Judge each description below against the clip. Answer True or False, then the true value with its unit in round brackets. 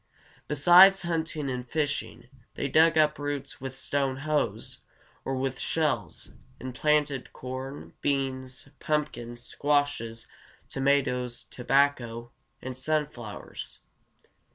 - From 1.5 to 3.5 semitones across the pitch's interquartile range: True (2.9 semitones)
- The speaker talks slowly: True (100 wpm)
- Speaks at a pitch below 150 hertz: True (135 Hz)